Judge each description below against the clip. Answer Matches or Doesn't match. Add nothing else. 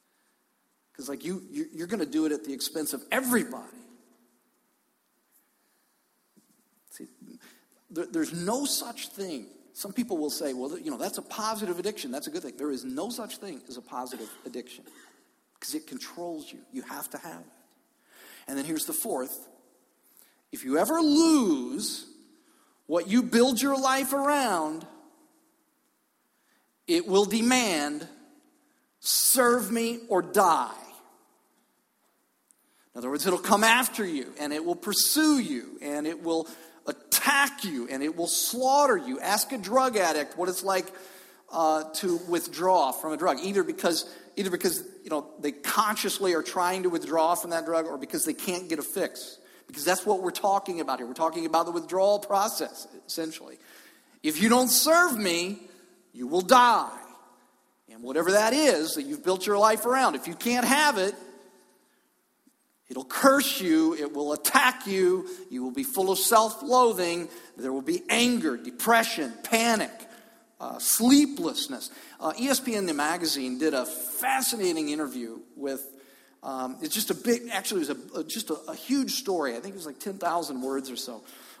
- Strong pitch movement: Matches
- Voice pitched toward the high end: Matches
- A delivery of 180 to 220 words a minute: Doesn't match